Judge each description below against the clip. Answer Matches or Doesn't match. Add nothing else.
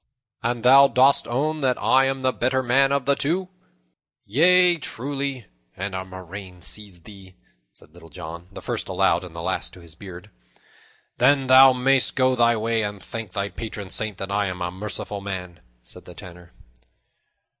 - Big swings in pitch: Matches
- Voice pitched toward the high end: Doesn't match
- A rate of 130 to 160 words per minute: Doesn't match